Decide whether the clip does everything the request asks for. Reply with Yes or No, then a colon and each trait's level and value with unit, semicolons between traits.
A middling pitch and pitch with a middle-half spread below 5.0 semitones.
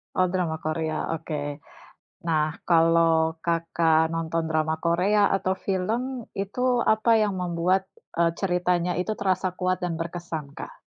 Yes: medium, 175 Hz; narrow, 2.6 semitones